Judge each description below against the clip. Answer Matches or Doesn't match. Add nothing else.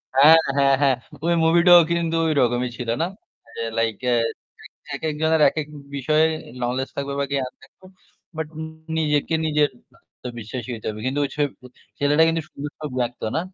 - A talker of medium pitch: Matches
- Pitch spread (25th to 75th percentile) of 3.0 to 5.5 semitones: Matches